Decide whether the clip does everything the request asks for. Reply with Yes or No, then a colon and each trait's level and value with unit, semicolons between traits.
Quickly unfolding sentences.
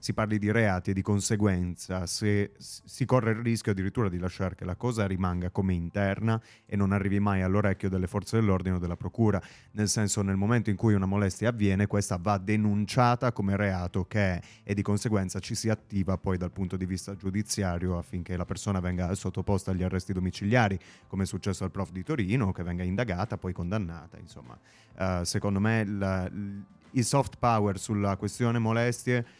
Yes: fast, 190 wpm